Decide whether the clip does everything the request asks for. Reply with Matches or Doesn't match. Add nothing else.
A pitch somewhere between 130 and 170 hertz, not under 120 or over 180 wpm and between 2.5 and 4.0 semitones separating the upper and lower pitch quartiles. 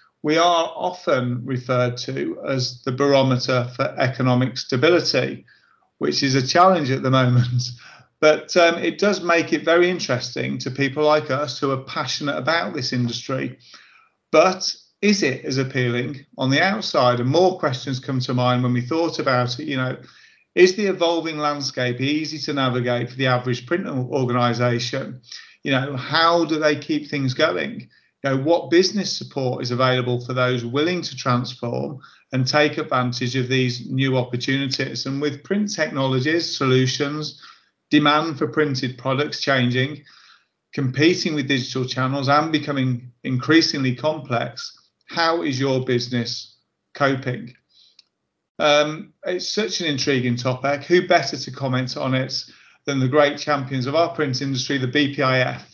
Matches